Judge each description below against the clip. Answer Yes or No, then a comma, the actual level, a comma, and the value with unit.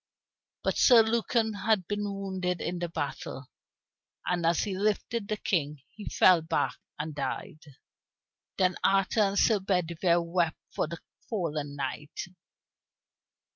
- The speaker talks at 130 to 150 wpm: Yes, slow, 135 wpm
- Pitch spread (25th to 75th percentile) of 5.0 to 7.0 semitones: No, average, 4.1 semitones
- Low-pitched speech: No, medium, 180 Hz